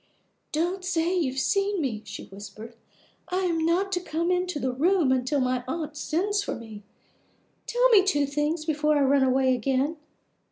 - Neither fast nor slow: Yes, average, 175 wpm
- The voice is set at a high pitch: Yes, very high, 305 Hz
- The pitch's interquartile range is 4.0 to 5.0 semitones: No, wide, 5.6 semitones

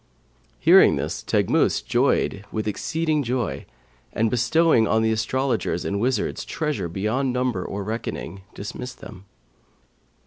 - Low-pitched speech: Yes, low, 115 Hz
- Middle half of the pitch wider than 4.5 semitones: No, average, 3.9 semitones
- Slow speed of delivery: Yes, slow, 125 wpm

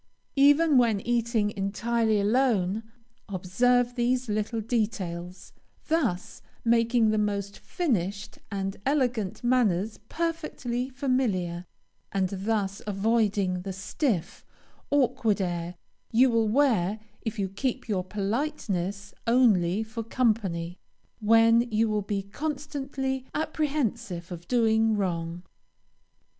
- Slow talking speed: Yes, slow, 105 wpm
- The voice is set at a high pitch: Yes, high, 220 Hz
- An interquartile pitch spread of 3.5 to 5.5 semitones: Yes, average, 4.1 semitones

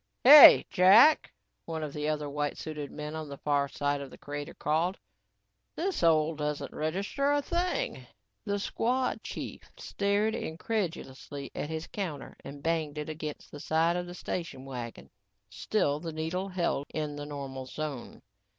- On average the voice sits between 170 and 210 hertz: No, medium, 155 Hz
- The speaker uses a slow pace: No, average, 160 wpm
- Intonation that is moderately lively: Yes, average, 4.4 semitones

